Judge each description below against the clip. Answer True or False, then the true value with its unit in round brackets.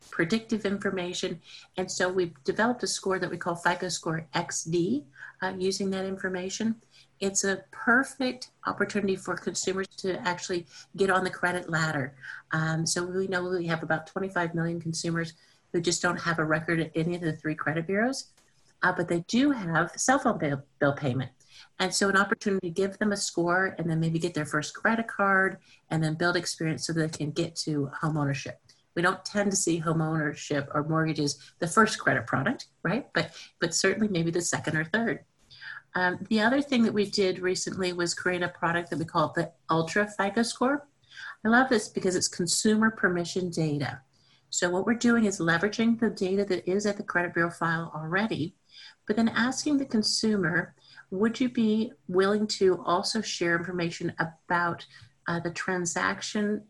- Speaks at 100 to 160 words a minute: False (185 wpm)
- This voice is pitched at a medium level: True (180 Hz)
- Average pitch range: True (3.4 semitones)